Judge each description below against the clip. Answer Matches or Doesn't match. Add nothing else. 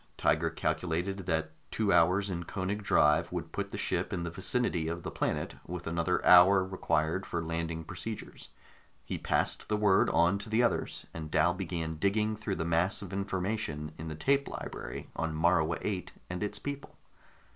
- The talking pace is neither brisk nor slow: Matches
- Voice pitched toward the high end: Doesn't match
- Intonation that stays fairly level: Doesn't match